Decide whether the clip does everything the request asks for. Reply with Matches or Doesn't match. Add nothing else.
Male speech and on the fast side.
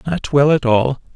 Matches